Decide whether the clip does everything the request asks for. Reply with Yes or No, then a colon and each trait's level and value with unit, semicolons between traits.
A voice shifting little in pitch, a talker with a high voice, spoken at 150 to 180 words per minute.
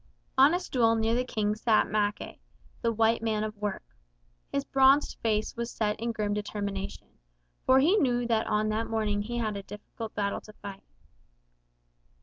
Yes: narrow, 2.3 semitones; high, 220 Hz; average, 170 wpm